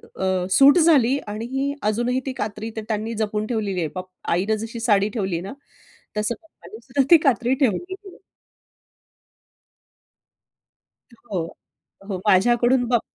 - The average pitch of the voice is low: No, high, 225 Hz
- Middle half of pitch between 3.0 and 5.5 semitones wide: Yes, average, 3.9 semitones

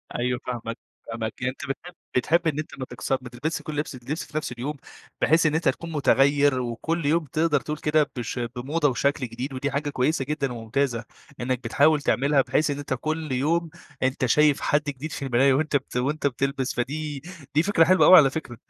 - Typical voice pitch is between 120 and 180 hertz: Yes, medium, 140 Hz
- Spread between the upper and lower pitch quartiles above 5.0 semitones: No, average, 3.4 semitones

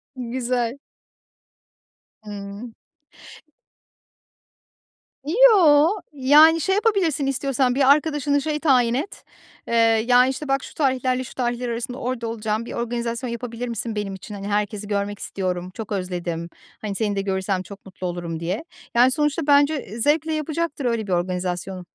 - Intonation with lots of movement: Yes, wide, 5.9 semitones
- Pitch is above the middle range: Yes, high, 240 Hz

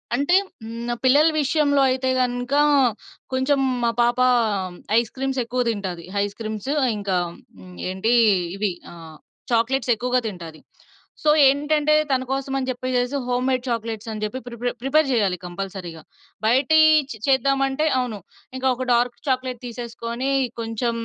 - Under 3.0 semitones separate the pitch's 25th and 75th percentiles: No, average, 3.4 semitones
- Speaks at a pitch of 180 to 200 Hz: No, high, 245 Hz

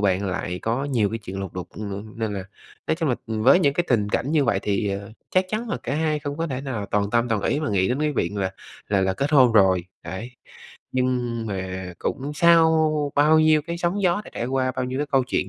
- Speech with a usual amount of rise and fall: No, wide, 6.6 semitones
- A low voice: Yes, low, 125 Hz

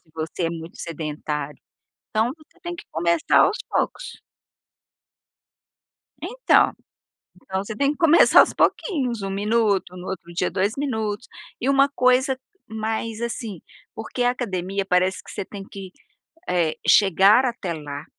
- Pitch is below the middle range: No, high, 205 Hz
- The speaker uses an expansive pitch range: Yes, wide, 5.7 semitones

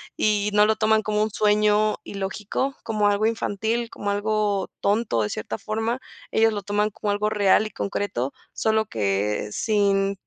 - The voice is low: No, high, 210 Hz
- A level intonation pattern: Yes, narrow, 1.4 semitones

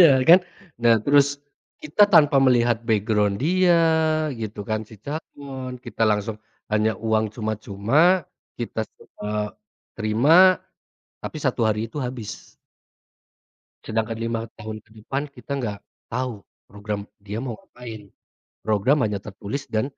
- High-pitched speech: No, low, 115 Hz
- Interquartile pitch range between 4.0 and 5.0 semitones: Yes, average, 4.3 semitones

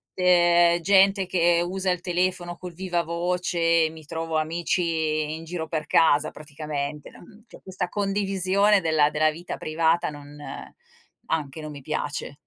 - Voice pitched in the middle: Yes, medium, 170 Hz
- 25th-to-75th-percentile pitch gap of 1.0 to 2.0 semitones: No, narrow, 2.6 semitones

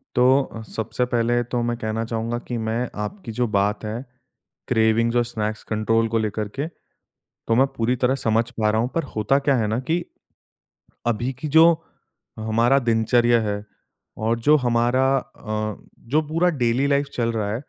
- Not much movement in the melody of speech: Yes, narrow, 2.2 semitones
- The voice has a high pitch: No, low, 115 Hz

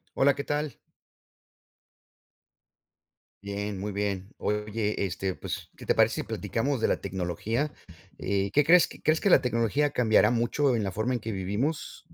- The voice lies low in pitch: Yes, low, 110 Hz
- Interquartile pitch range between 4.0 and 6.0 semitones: Yes, wide, 5.6 semitones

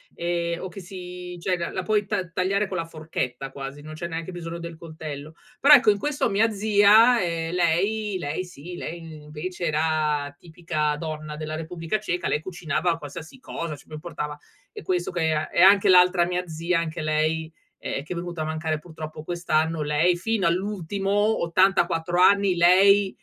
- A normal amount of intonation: Yes, average, 3.0 semitones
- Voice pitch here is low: No, medium, 170 Hz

